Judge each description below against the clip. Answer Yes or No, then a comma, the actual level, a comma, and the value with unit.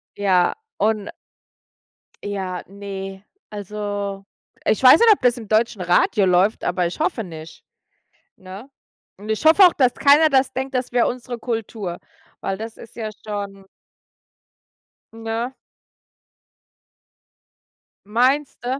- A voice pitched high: Yes, high, 215 Hz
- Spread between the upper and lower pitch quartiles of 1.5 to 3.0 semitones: No, average, 4.2 semitones